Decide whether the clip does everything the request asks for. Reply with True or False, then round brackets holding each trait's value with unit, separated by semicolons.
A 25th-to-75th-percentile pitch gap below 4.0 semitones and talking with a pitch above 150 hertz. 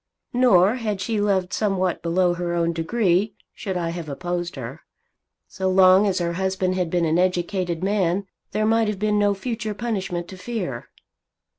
True (3.1 semitones; 185 Hz)